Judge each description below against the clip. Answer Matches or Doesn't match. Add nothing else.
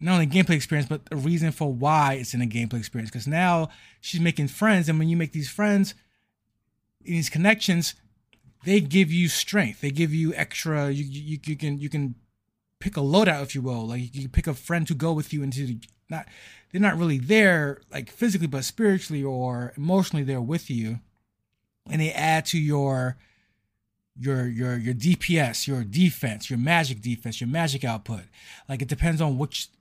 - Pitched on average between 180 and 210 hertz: Doesn't match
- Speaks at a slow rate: Doesn't match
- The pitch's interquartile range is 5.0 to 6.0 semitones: Matches